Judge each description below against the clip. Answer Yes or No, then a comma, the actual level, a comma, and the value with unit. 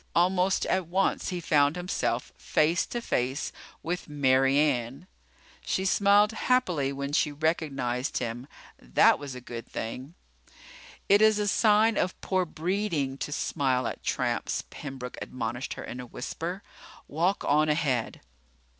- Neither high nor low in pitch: Yes, medium, 150 Hz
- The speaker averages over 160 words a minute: No, average, 140 wpm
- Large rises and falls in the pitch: Yes, wide, 5.8 semitones